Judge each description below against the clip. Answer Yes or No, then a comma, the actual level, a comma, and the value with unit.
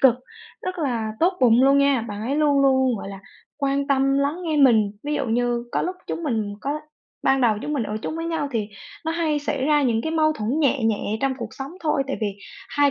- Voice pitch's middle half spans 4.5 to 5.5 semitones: No, average, 4.1 semitones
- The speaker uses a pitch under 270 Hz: No, very high, 275 Hz